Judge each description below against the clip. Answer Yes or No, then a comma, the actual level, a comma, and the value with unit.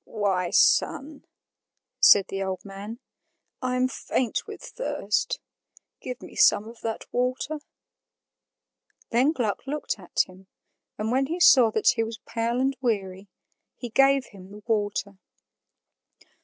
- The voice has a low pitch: No, high, 230 Hz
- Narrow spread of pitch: No, average, 4.1 semitones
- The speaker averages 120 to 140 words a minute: Yes, slow, 135 wpm